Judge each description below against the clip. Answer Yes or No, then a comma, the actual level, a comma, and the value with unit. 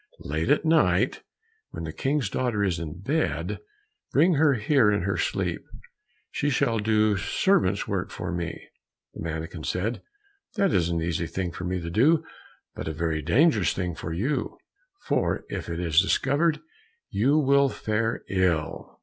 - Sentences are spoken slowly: No, average, 160 wpm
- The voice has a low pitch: Yes, low, 100 Hz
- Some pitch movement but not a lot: No, wide, 8.1 semitones